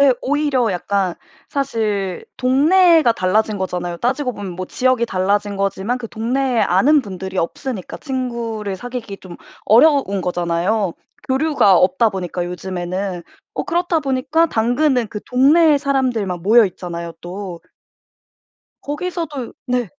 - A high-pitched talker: Yes, high, 225 Hz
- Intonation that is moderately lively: No, wide, 6.0 semitones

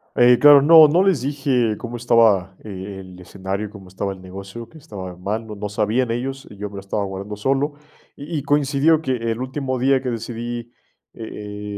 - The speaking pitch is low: Yes, low, 115 Hz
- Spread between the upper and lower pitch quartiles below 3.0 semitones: No, average, 5.0 semitones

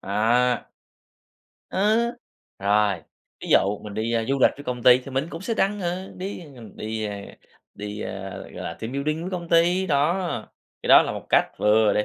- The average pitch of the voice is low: Yes, low, 125 Hz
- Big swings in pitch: Yes, wide, 8.2 semitones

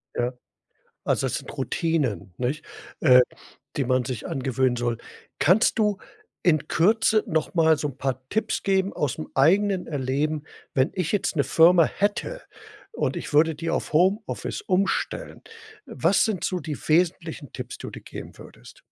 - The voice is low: No, medium, 160 Hz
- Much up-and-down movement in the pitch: Yes, wide, 6.0 semitones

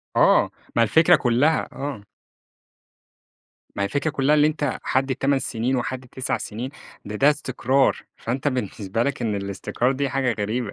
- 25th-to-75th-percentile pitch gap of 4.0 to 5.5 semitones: No, average, 3.3 semitones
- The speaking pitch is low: Yes, low, 130 Hz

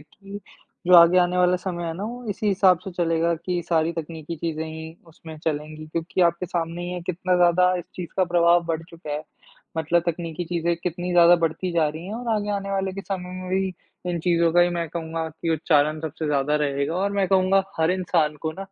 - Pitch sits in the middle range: Yes, medium, 170 Hz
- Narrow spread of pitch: Yes, narrow, 2.2 semitones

